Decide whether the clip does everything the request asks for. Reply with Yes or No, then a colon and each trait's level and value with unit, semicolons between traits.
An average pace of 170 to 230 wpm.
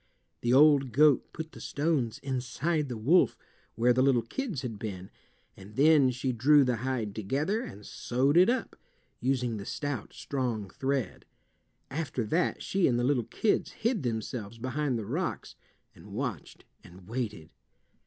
No: average, 155 wpm